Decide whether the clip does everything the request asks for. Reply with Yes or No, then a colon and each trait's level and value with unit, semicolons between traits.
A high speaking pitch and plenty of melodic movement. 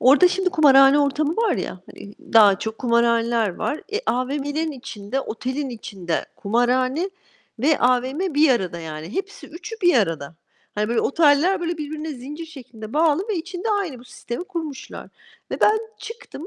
Yes: very high, 275 Hz; wide, 5.8 semitones